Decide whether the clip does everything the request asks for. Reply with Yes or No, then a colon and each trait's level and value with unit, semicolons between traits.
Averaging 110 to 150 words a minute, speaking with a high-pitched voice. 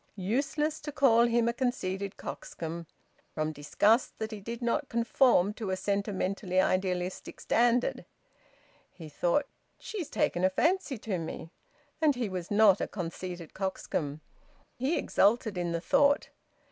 Yes: average, 140 wpm; high, 205 Hz